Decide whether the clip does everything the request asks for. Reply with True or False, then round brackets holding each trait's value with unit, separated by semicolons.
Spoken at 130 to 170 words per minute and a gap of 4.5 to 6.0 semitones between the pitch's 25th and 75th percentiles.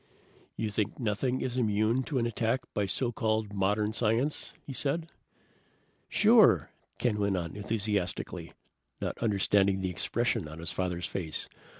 False (140 wpm; 3.7 semitones)